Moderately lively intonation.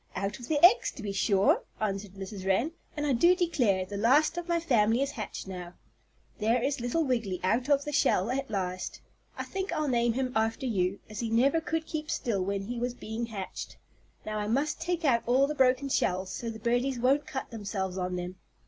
No: wide, 5.7 semitones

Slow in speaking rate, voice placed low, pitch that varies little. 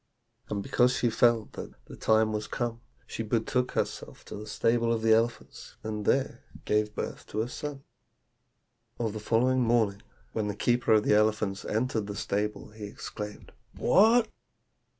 No: average, 165 wpm; low, 110 Hz; narrow, 2.1 semitones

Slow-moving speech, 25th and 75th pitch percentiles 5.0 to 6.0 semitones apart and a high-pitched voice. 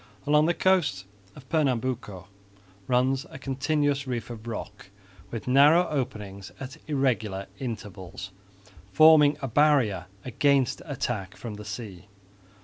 No: slow, 120 wpm; average, 5.3 semitones; low, 130 Hz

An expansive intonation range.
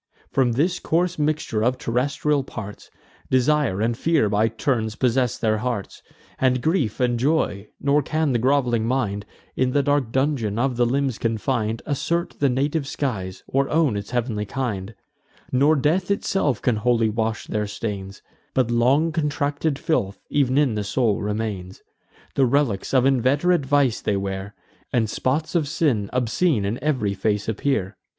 No: average, 4.7 semitones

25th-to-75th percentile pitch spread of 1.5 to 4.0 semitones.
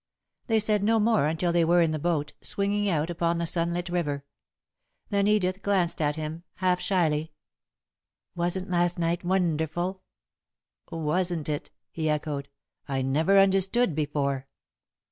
Yes: average, 3.4 semitones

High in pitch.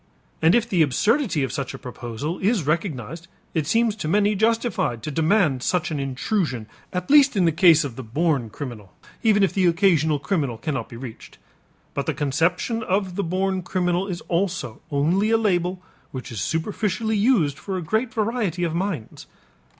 No: medium, 175 Hz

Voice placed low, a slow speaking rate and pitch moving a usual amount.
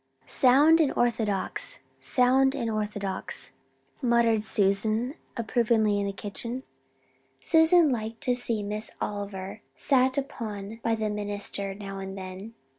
No: high, 220 Hz; slow, 120 wpm; average, 3.5 semitones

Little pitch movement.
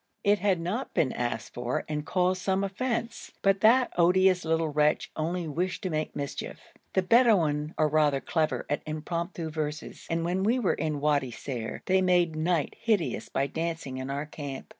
No: average, 4.0 semitones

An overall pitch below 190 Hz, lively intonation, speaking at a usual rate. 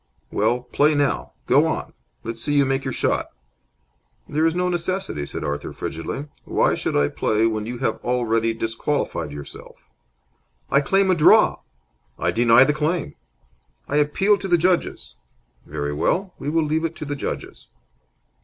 Yes: medium, 140 Hz; wide, 6.2 semitones; average, 165 wpm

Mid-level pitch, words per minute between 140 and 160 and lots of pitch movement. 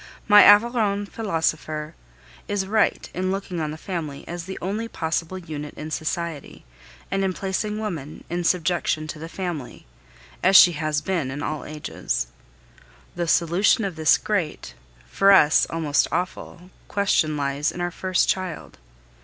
No: medium, 175 Hz; average, 150 wpm; average, 3.8 semitones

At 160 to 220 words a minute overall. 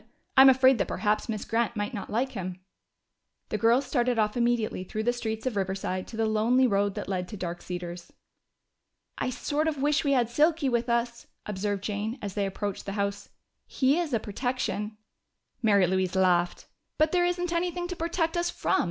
Yes: average, 190 wpm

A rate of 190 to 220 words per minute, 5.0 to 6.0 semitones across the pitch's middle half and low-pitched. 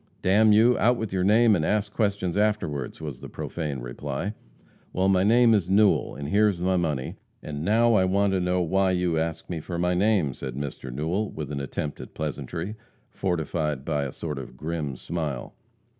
Yes: average, 195 wpm; wide, 5.4 semitones; very low, 90 Hz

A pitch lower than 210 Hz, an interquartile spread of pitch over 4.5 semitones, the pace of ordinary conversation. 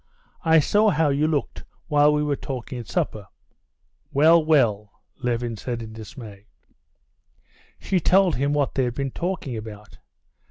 Yes: medium, 140 Hz; average, 5.1 semitones; average, 150 wpm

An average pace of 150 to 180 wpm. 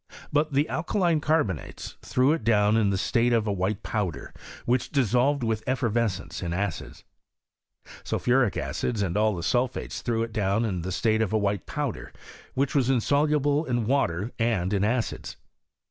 Yes: average, 165 wpm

